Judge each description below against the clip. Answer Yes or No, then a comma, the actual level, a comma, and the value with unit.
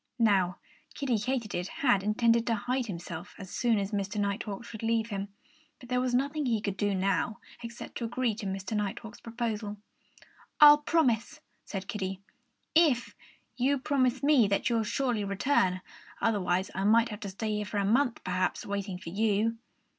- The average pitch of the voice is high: Yes, high, 220 Hz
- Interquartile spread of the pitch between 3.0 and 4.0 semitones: Yes, average, 3.6 semitones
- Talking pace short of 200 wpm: Yes, average, 170 wpm